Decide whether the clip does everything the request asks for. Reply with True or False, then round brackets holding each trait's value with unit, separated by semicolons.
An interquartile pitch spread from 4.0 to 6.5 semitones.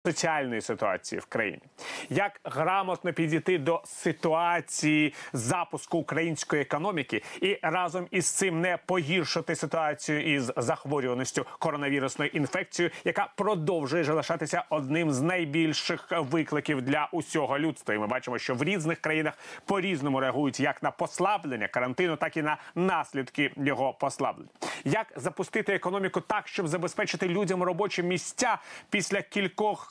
False (3.6 semitones)